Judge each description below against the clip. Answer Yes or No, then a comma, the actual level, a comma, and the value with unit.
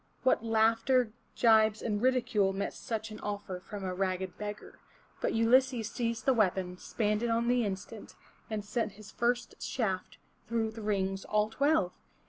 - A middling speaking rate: Yes, average, 160 wpm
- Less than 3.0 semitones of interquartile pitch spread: Yes, narrow, 2.6 semitones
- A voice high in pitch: Yes, high, 220 Hz